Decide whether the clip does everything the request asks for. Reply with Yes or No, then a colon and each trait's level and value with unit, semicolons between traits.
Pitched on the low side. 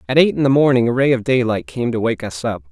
Yes: low, 120 Hz